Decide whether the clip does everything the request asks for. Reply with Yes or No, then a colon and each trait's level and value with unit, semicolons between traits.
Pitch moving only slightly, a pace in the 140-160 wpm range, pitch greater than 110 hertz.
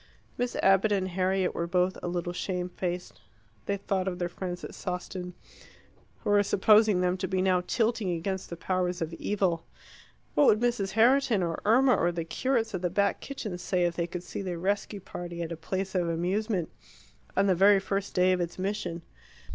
No: narrow, 2.3 semitones; average, 195 wpm; medium, 185 Hz